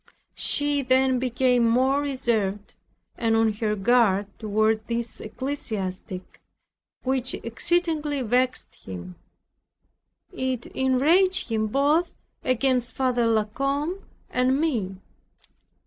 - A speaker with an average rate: No, slow, 100 wpm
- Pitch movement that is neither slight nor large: Yes, average, 3.9 semitones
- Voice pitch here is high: Yes, very high, 250 Hz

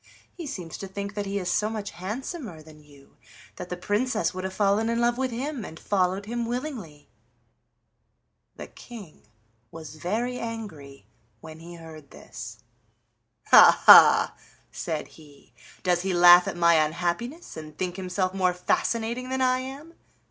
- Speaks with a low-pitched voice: No, high, 190 Hz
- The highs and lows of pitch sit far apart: Yes, wide, 5.9 semitones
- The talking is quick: No, average, 155 wpm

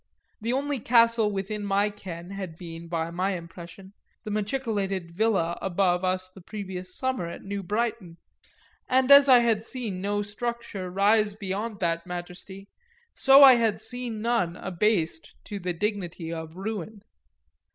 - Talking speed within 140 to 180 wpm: Yes, average, 150 wpm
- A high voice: Yes, high, 200 Hz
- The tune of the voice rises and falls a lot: No, average, 3.9 semitones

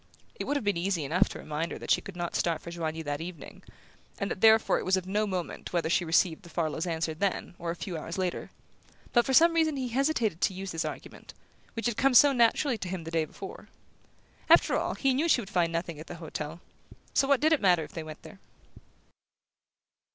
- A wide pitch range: Yes, wide, 5.8 semitones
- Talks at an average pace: No, fast, 230 wpm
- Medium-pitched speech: Yes, medium, 180 Hz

